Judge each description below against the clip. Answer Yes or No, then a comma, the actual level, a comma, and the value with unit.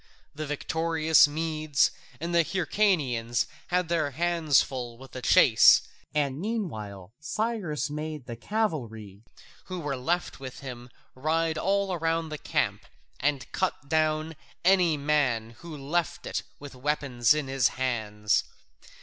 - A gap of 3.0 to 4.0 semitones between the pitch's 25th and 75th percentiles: No, average, 4.5 semitones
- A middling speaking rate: No, slow, 130 wpm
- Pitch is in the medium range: Yes, medium, 150 Hz